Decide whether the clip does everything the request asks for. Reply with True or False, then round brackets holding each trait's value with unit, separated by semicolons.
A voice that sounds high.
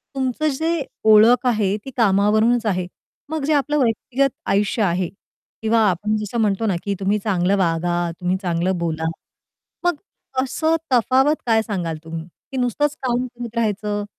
True (215 Hz)